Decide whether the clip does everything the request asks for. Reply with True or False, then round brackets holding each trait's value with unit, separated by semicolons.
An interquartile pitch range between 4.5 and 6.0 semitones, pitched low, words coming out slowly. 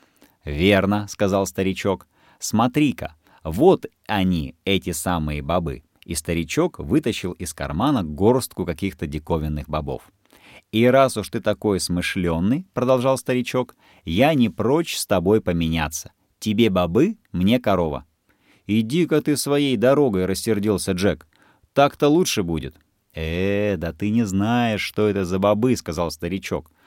False (5.0 semitones; 95 Hz; 125 wpm)